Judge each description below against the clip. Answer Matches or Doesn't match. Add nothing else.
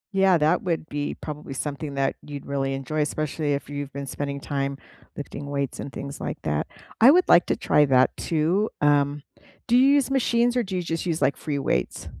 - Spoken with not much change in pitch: Doesn't match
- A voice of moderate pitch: Matches